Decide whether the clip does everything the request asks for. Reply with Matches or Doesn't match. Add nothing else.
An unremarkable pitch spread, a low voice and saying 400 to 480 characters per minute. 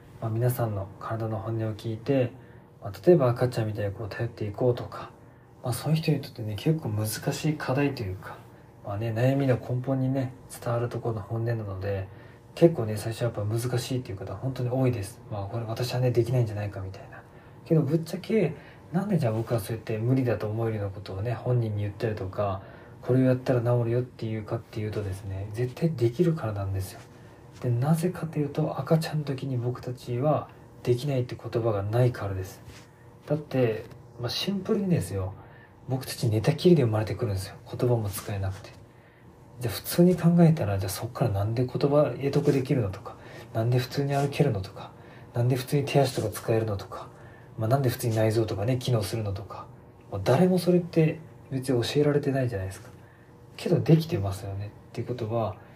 Matches